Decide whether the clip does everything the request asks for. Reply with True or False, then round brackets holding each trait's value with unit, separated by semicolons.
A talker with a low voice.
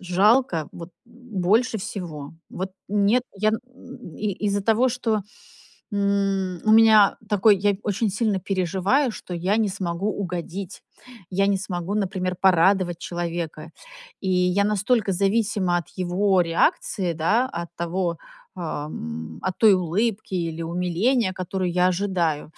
False (190 Hz)